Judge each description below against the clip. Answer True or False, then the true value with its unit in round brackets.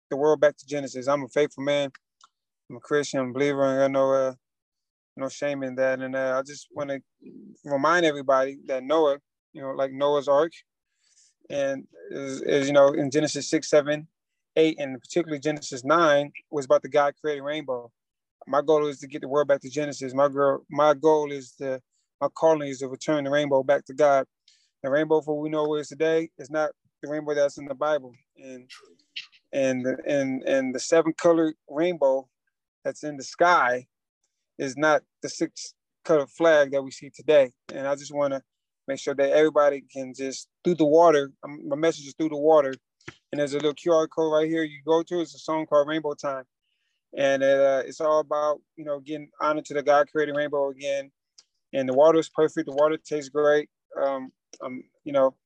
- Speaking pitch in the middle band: True (145 Hz)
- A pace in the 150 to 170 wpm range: False (205 wpm)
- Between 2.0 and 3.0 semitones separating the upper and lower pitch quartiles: True (2.4 semitones)